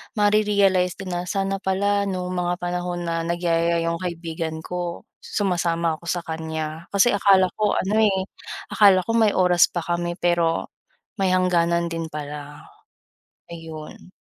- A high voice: No, medium, 175 Hz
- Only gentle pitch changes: Yes, narrow, 2.3 semitones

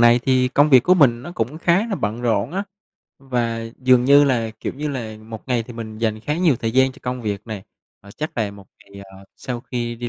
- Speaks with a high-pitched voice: No, low, 120 Hz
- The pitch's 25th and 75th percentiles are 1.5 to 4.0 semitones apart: Yes, average, 3.4 semitones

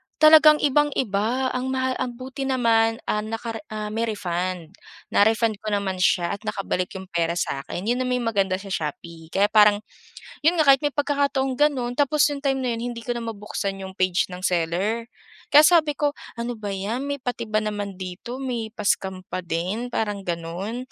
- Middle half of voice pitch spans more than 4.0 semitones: Yes, average, 5.0 semitones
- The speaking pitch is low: No, high, 225 Hz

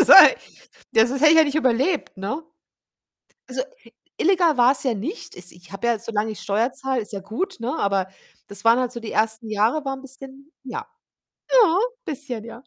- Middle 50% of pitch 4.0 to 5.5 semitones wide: Yes, average, 4.8 semitones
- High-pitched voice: Yes, high, 245 Hz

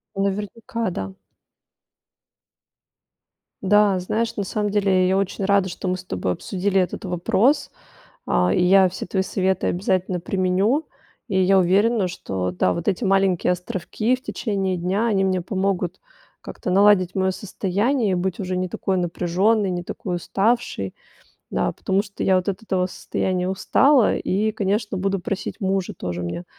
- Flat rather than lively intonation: Yes, narrow, 2.0 semitones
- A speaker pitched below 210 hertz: Yes, high, 190 Hz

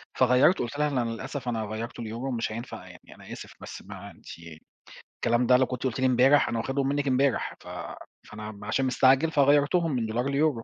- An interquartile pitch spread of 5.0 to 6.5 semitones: No, average, 3.1 semitones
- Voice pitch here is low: Yes, low, 130 Hz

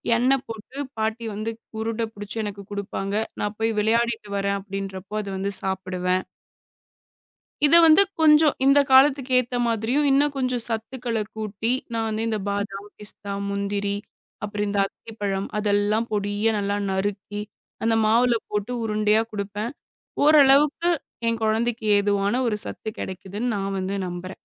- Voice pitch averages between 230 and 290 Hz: No, high, 215 Hz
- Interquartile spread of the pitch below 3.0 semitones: Yes, narrow, 2.6 semitones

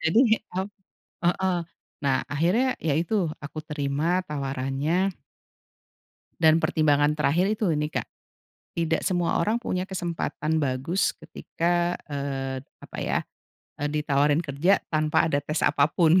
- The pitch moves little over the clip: No, average, 3.6 semitones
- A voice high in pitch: No, medium, 155 Hz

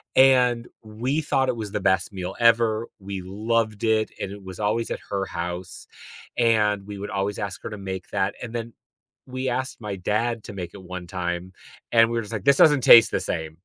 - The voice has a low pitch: Yes, low, 105 Hz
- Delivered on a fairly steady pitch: No, average, 3.4 semitones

